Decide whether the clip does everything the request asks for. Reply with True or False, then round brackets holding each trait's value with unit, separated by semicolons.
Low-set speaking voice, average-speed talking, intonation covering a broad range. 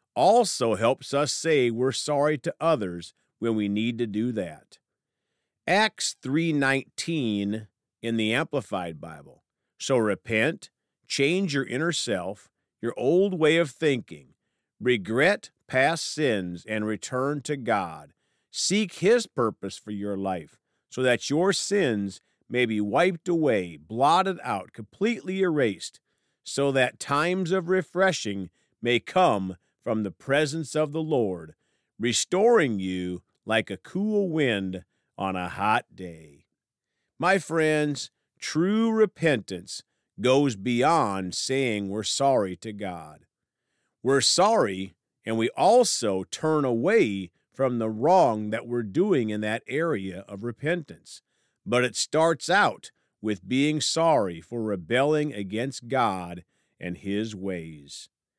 False (125 Hz; 125 wpm; 7.5 semitones)